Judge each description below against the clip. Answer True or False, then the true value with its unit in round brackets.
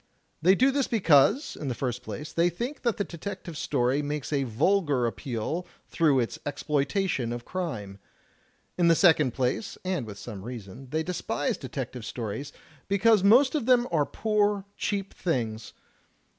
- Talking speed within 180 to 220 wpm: False (155 wpm)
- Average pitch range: False (7.8 semitones)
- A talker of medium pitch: True (150 Hz)